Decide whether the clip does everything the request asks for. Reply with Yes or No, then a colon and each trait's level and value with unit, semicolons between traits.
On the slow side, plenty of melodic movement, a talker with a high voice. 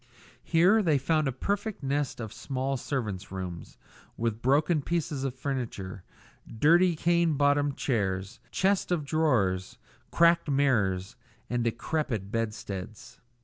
No: slow, 120 wpm; wide, 6.5 semitones; low, 135 Hz